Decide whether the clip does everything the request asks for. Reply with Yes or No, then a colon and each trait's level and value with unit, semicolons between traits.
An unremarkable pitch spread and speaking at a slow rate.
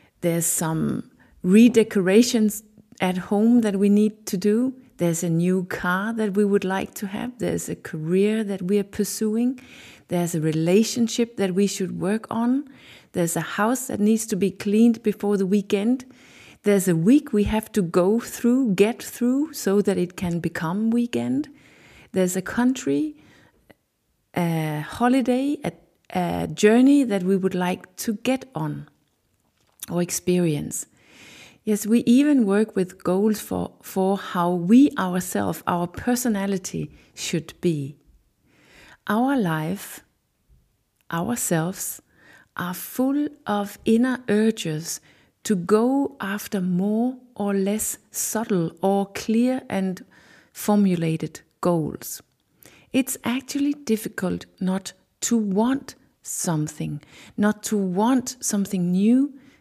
Yes: average, 4.7 semitones; slow, 125 wpm